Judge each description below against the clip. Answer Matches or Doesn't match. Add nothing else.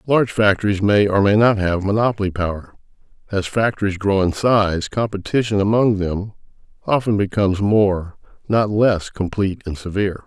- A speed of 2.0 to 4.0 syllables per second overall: Doesn't match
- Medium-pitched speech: Doesn't match